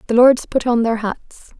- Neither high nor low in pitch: No, high, 235 Hz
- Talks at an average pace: No, fast, 225 wpm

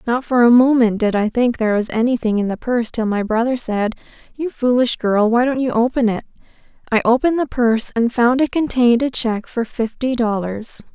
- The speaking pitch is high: Yes, high, 235 Hz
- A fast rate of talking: Yes, fast, 210 wpm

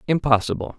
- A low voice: Yes, low, 130 Hz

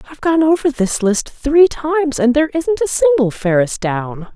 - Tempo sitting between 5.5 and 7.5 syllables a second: No, 5.0 syllables/s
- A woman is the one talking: Yes, female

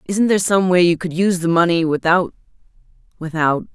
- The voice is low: No, medium, 175 Hz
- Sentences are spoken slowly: No, average, 160 wpm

